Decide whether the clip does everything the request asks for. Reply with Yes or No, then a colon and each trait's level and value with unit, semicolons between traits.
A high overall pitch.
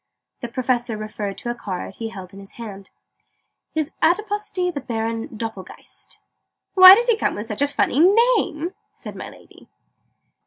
Yes: high, 240 Hz